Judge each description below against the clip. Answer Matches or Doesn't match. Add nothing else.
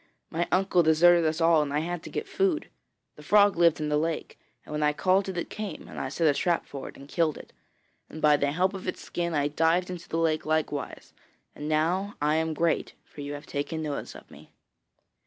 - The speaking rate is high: Matches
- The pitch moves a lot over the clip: Doesn't match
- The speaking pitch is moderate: Matches